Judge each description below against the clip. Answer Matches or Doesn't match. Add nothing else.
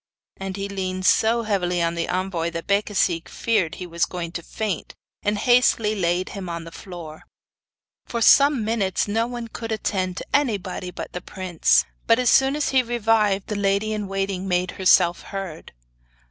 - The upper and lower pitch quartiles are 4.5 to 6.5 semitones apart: Doesn't match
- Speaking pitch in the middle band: Doesn't match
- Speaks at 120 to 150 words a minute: Doesn't match